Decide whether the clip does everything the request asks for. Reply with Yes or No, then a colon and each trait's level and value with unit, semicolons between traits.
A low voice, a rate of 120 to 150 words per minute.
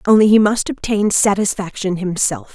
No: high, 195 Hz; average, 140 wpm